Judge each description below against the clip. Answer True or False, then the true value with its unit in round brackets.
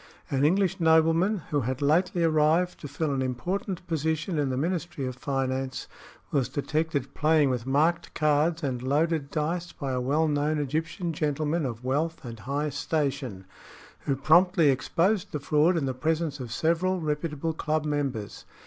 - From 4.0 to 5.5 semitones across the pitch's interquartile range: False (3.2 semitones)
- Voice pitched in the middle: True (150 Hz)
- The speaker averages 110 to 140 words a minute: False (160 wpm)